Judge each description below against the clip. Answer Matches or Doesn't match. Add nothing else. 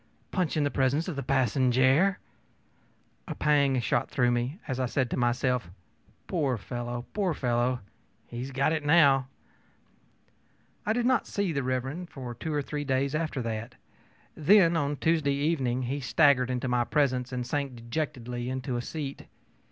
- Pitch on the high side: Doesn't match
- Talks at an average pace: Matches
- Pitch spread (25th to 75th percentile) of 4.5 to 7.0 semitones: Doesn't match